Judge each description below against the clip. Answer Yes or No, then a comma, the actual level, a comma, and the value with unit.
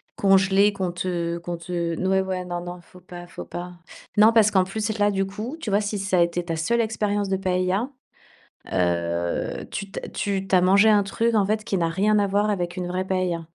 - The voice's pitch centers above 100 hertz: Yes, high, 190 Hz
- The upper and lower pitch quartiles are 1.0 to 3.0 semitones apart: Yes, average, 2.7 semitones